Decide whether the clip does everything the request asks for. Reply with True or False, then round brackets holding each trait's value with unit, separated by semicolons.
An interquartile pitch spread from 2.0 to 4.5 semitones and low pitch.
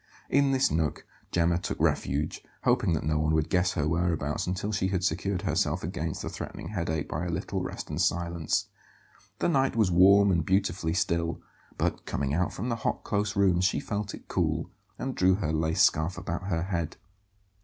True (3.4 semitones; 90 Hz)